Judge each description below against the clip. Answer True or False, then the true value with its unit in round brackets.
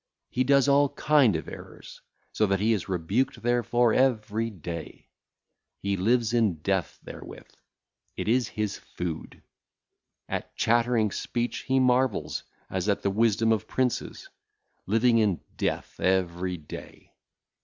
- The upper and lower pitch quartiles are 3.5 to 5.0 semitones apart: True (4.2 semitones)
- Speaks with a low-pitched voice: True (110 Hz)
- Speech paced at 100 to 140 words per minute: True (135 wpm)